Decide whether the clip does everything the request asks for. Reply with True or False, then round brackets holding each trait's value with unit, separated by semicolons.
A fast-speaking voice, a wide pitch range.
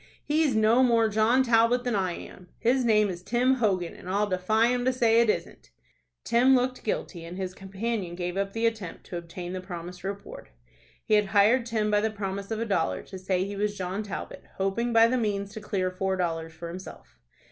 False (210 wpm; 3.8 semitones)